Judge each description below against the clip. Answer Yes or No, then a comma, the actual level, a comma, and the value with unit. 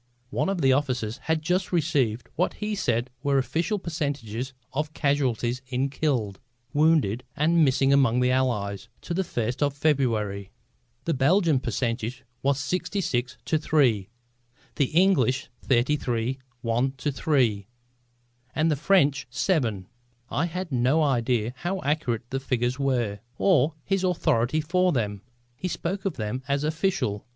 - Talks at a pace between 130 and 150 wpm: Yes, average, 140 wpm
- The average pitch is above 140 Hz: No, low, 135 Hz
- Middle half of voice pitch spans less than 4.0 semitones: No, average, 4.7 semitones